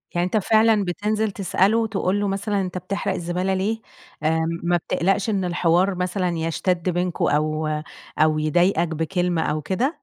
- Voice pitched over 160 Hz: Yes, medium, 185 Hz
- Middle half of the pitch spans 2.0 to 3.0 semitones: Yes, narrow, 2.6 semitones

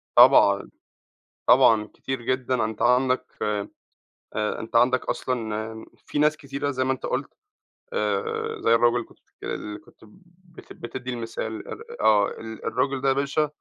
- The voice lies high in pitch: No, low, 130 Hz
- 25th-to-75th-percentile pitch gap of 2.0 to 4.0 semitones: Yes, average, 3.5 semitones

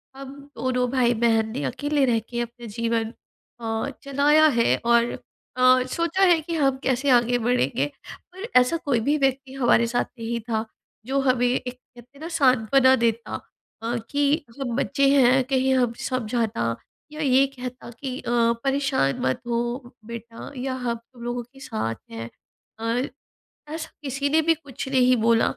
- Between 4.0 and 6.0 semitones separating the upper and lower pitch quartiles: No, average, 2.7 semitones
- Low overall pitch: No, very high, 250 Hz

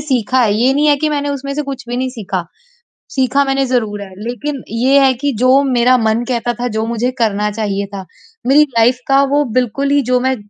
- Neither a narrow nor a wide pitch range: Yes, average, 3.5 semitones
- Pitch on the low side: No, very high, 255 Hz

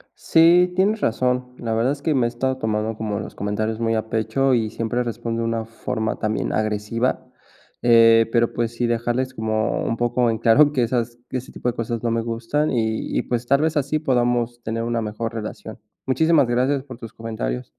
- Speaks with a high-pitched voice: No, low, 120 Hz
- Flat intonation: Yes, narrow, 2.2 semitones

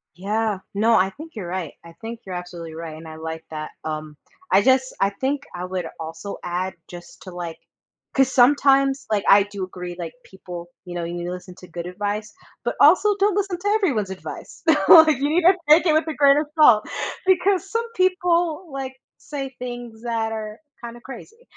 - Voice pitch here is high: Yes, high, 220 Hz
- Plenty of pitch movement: Yes, wide, 8.6 semitones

